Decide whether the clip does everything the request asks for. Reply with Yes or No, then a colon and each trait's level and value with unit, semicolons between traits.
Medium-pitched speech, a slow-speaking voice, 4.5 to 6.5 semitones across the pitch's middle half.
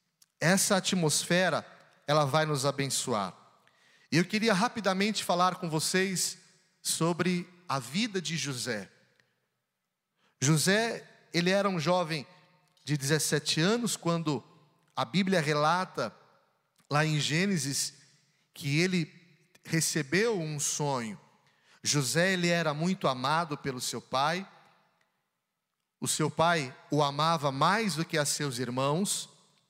No: medium, 165 Hz; slow, 115 wpm; average, 3.6 semitones